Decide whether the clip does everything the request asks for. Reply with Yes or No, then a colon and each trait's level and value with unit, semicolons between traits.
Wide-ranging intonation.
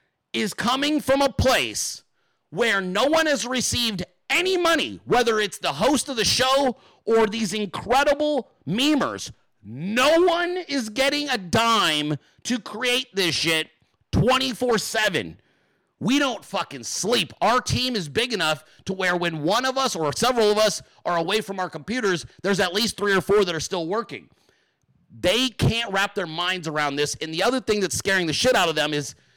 Yes: wide, 6.5 semitones